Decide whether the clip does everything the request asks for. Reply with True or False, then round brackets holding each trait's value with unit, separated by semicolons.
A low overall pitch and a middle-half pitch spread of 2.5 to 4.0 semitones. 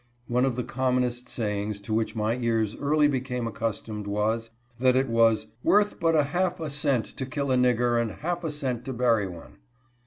True (125 Hz; 3.6 semitones)